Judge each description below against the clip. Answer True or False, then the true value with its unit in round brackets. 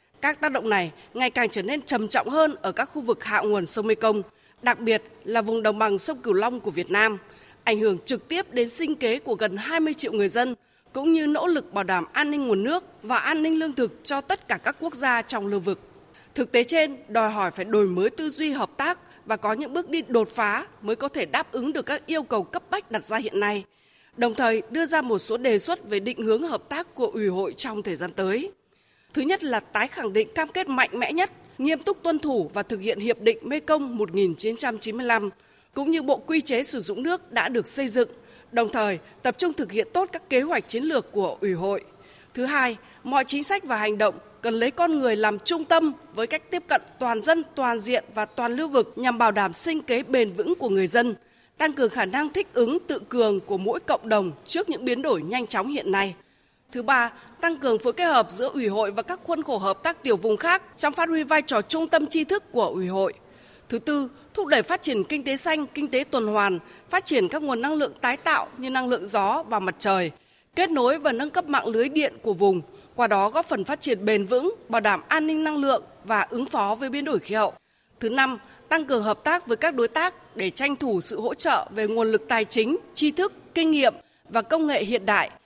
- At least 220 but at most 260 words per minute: True (245 wpm)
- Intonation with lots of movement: True (6.4 semitones)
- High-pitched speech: True (255 Hz)